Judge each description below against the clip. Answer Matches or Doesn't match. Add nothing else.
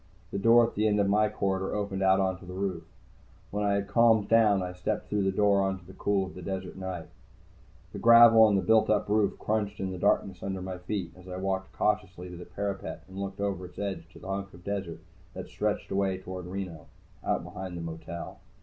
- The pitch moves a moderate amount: Doesn't match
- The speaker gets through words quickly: Matches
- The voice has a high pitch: Doesn't match